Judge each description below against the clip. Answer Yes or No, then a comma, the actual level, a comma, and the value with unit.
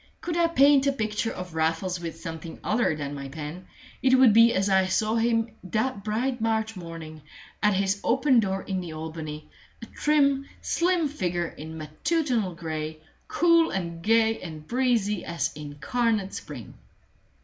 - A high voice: Yes, high, 200 Hz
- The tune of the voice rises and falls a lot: Yes, wide, 6.7 semitones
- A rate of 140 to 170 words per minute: Yes, average, 160 wpm